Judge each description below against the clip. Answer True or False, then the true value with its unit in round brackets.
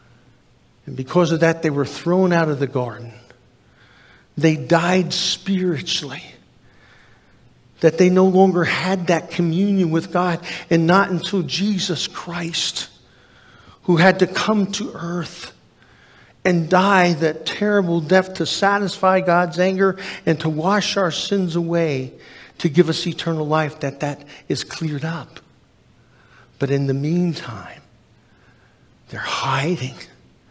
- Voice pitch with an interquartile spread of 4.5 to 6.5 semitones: False (4.1 semitones)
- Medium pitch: True (170 Hz)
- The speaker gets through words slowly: True (130 wpm)